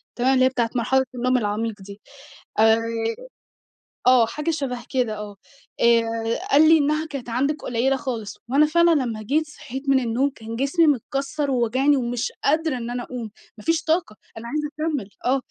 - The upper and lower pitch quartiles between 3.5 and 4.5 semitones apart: Yes, average, 4.1 semitones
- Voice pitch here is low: No, very high, 255 Hz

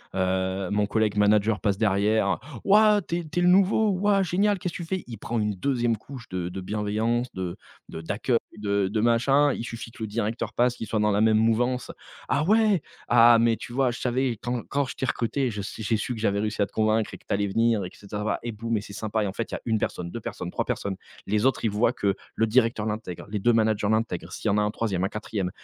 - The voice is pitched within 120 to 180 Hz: No, low, 110 Hz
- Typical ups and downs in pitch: Yes, average, 3.0 semitones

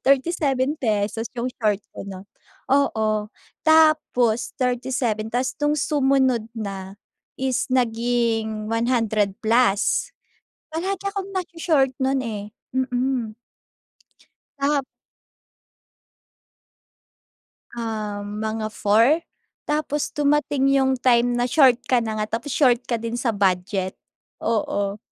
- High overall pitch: Yes, high, 240 Hz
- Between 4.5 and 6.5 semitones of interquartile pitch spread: No, average, 3.8 semitones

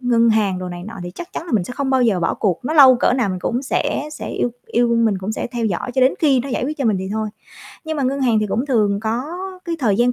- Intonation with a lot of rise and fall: No, average, 3.9 semitones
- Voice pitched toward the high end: Yes, high, 235 Hz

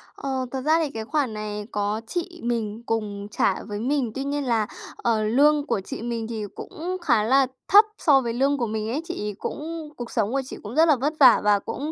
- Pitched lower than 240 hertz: No, high, 245 Hz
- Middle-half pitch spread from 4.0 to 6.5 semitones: Yes, average, 5.1 semitones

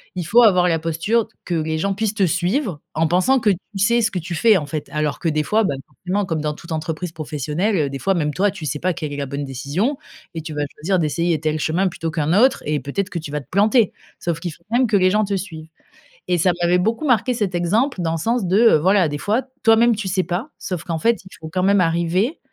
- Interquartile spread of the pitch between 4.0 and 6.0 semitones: Yes, average, 4.7 semitones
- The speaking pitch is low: No, medium, 180 Hz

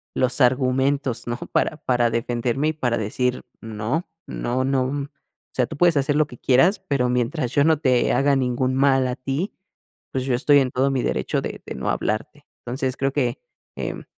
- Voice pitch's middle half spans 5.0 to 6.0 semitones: No, narrow, 2.4 semitones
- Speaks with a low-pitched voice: Yes, low, 130 Hz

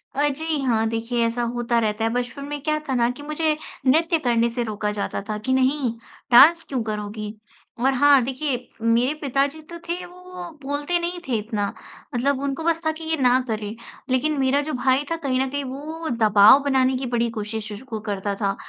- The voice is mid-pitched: No, very high, 260 Hz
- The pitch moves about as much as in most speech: Yes, average, 4.2 semitones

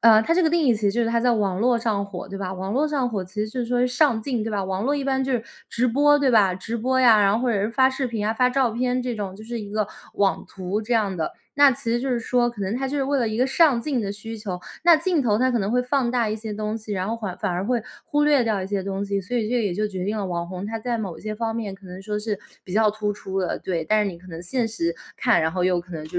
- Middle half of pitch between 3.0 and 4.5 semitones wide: Yes, average, 4.0 semitones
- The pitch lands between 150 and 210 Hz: No, high, 220 Hz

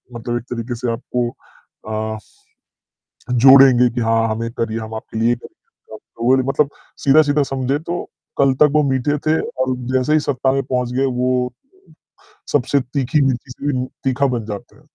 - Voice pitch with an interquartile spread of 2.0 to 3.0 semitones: Yes, narrow, 2.6 semitones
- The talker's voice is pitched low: Yes, low, 130 Hz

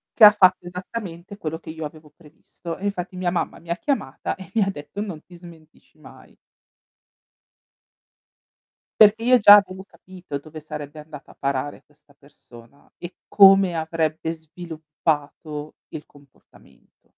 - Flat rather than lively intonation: No, average, 3.7 semitones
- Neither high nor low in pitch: Yes, medium, 165 Hz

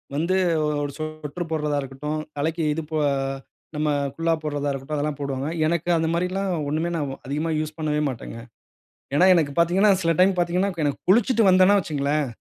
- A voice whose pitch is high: No, medium, 155 Hz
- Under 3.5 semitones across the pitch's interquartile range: Yes, average, 3.0 semitones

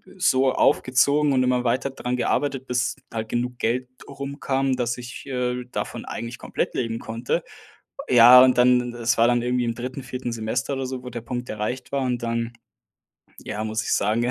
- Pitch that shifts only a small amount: Yes, narrow, 1.6 semitones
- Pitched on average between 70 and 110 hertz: No, low, 125 Hz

